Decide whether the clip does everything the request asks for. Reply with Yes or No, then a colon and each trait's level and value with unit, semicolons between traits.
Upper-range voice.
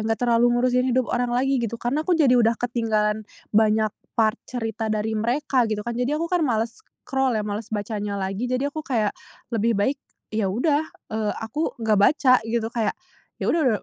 Yes: high, 230 Hz